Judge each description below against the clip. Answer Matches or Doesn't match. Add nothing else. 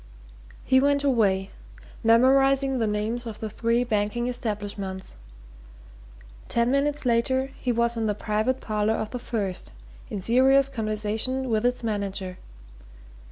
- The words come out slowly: Matches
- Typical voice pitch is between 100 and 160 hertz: Doesn't match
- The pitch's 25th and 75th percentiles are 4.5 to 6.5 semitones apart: Doesn't match